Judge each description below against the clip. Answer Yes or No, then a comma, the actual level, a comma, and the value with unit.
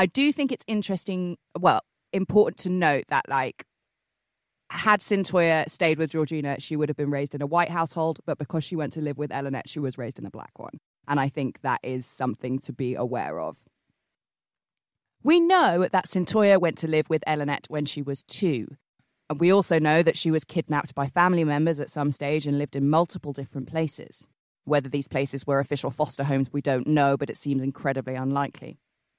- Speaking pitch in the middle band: Yes, medium, 150 Hz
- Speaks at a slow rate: No, average, 200 wpm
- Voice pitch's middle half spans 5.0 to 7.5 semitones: No, average, 3.4 semitones